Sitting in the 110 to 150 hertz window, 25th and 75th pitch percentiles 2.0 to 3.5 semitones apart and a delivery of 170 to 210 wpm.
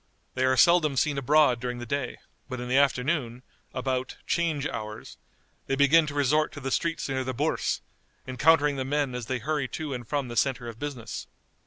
Yes: low, 135 Hz; average, 2.9 semitones; average, 195 wpm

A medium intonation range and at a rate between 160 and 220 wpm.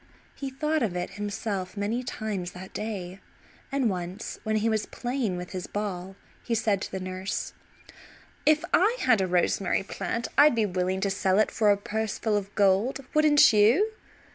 Yes: average, 3.8 semitones; average, 180 wpm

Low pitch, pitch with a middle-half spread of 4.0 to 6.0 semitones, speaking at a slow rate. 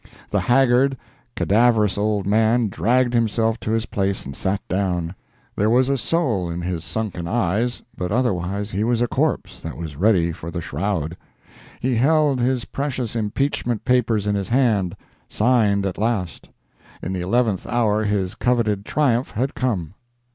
No: low, 110 Hz; average, 4.3 semitones; average, 160 wpm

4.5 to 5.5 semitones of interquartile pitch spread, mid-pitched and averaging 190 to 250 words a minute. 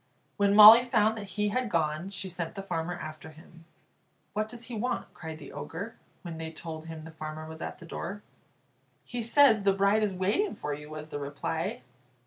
Yes: average, 4.9 semitones; medium, 180 Hz; average, 200 wpm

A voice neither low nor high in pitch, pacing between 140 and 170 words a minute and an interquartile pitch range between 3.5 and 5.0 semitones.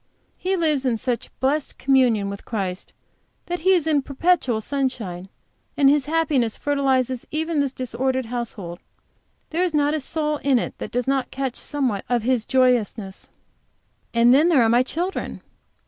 No: very high, 265 Hz; average, 160 wpm; average, 4.0 semitones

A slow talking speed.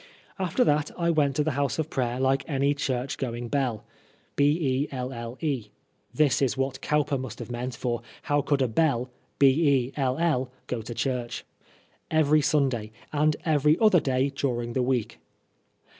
No: average, 145 wpm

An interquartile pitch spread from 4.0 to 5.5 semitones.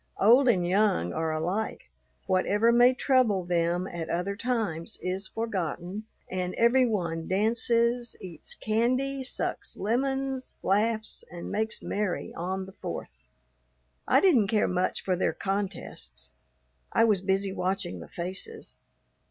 Yes: average, 4.5 semitones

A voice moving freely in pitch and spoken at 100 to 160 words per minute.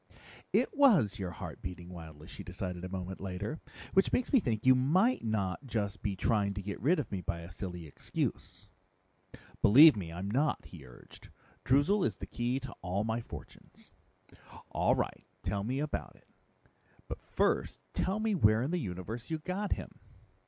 No: wide, 7.9 semitones; average, 180 wpm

